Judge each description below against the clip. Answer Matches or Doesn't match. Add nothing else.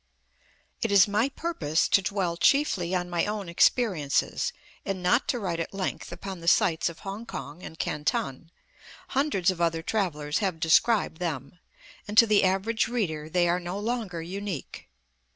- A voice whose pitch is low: Doesn't match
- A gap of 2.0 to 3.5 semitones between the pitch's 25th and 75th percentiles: Doesn't match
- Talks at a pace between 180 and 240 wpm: Doesn't match